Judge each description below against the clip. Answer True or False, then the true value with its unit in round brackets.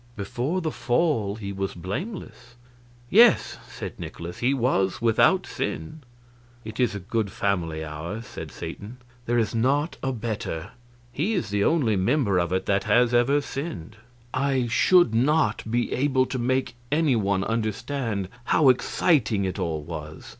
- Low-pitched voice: True (115 Hz)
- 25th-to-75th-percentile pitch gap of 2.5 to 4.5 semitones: False (5.3 semitones)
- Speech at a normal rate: True (155 wpm)